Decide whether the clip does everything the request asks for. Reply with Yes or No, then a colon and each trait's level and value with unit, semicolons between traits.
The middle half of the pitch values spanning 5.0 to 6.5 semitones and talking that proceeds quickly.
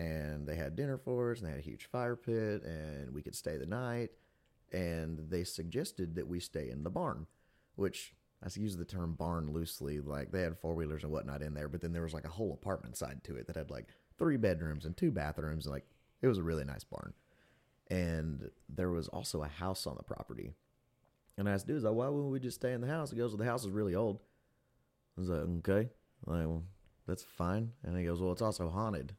Yes: average, 5.3 semitones; fast, 240 wpm